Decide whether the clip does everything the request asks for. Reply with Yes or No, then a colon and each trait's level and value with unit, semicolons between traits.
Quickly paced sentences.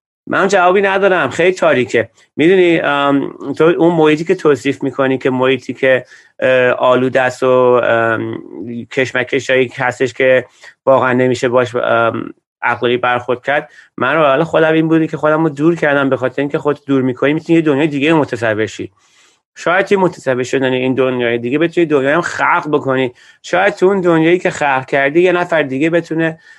Yes: fast, 160 wpm